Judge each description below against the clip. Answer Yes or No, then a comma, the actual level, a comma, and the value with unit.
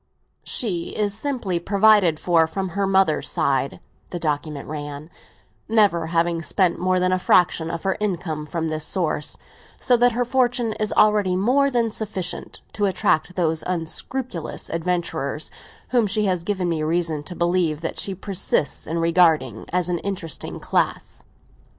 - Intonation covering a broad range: No, average, 3.9 semitones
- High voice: No, medium, 180 Hz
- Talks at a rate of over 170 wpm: No, average, 155 wpm